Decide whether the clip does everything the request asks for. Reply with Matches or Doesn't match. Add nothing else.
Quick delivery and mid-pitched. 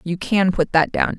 Matches